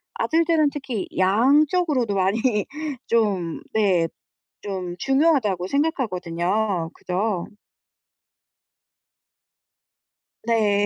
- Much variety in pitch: Yes, wide, 6.5 semitones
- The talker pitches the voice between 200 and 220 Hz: Yes, high, 215 Hz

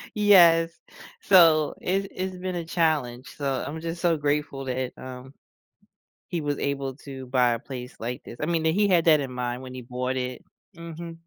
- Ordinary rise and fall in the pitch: Yes, average, 4.6 semitones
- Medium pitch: Yes, medium, 145 Hz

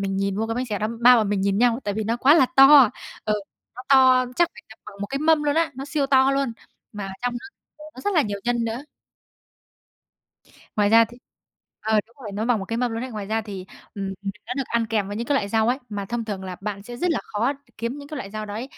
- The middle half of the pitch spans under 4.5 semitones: Yes, average, 4.1 semitones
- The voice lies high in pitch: Yes, high, 230 Hz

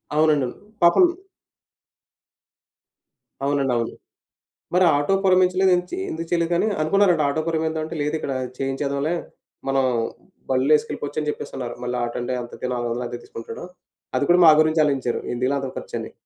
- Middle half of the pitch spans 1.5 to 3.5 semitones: No, average, 4.1 semitones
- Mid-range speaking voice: Yes, medium, 145 Hz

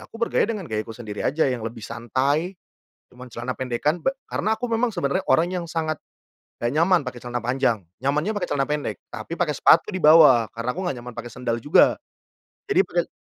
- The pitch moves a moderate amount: No, wide, 6.4 semitones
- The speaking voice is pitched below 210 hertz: Yes, medium, 140 Hz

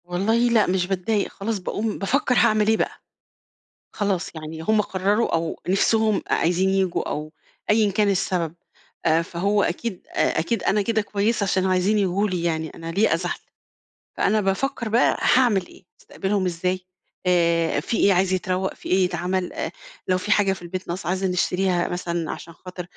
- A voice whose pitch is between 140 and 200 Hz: Yes, high, 190 Hz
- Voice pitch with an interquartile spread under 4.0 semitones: Yes, average, 2.8 semitones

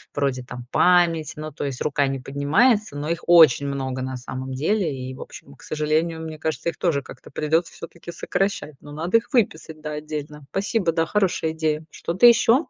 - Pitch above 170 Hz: No, medium, 155 Hz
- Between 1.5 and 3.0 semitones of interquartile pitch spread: No, average, 3.4 semitones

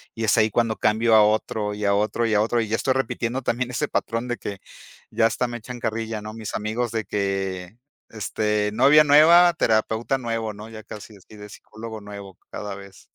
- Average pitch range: No, narrow, 2.1 semitones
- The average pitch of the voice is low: Yes, low, 110 Hz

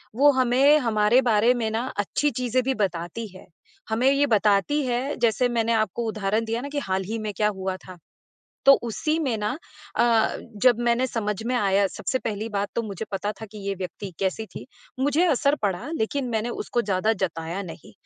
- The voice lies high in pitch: Yes, high, 225 Hz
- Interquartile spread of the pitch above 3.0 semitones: Yes, average, 3.8 semitones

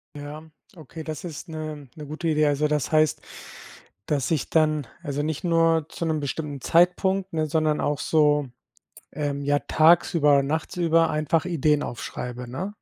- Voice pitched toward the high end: No, medium, 155 Hz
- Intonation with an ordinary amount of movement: No, narrow, 2.0 semitones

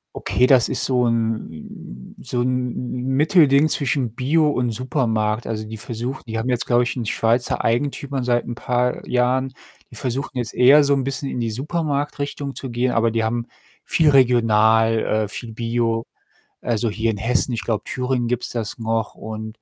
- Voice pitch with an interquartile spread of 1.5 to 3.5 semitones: Yes, average, 2.7 semitones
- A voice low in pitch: Yes, low, 120 Hz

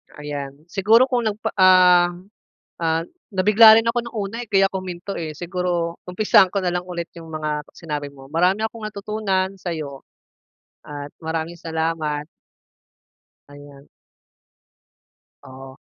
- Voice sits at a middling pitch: Yes, medium, 175 Hz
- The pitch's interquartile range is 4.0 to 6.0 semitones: Yes, average, 4.3 semitones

